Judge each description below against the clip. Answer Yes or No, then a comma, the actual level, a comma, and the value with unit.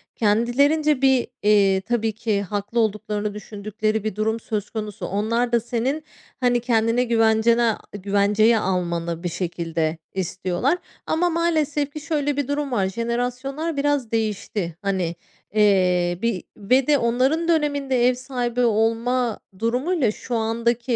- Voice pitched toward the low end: No, high, 230 Hz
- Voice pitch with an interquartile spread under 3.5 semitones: No, average, 3.8 semitones